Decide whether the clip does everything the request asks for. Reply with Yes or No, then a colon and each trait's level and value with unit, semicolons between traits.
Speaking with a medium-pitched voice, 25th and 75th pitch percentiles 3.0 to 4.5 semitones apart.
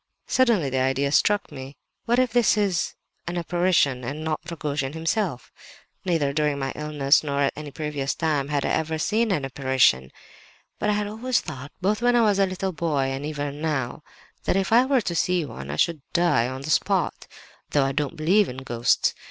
No: medium, 155 Hz; wide, 5.5 semitones